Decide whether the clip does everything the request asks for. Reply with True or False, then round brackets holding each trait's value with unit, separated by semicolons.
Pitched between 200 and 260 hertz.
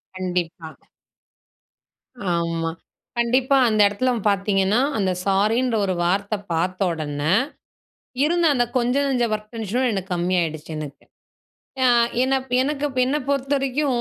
True (210 Hz)